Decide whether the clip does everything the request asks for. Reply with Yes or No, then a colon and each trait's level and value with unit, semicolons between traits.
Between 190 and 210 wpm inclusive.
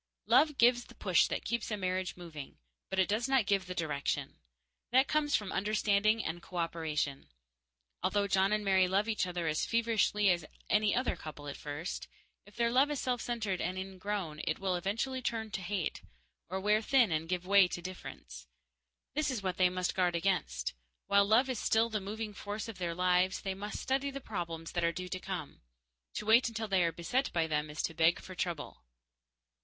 Yes: average, 200 wpm